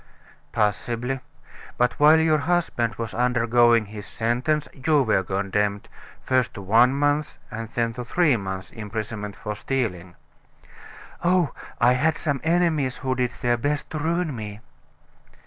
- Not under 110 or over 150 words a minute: Yes, average, 140 wpm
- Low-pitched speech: Yes, low, 120 Hz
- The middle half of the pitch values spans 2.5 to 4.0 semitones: No, average, 5.2 semitones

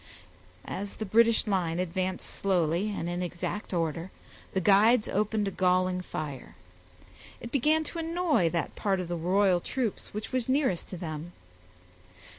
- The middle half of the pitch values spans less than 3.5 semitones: No, average, 3.9 semitones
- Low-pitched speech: No, high, 190 Hz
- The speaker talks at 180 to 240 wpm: No, average, 150 wpm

